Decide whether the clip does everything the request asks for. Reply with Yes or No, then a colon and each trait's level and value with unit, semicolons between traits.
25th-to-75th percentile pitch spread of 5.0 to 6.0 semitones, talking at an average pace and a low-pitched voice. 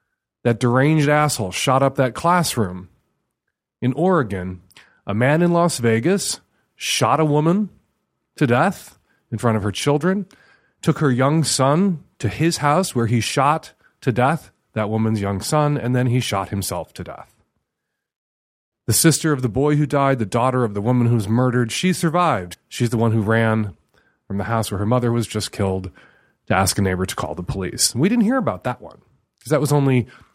Yes: wide, 5.6 semitones; average, 190 wpm; low, 125 Hz